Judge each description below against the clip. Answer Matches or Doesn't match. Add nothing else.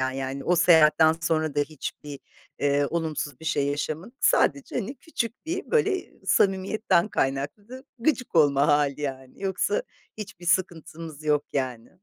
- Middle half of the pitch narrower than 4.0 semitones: Doesn't match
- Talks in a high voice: Doesn't match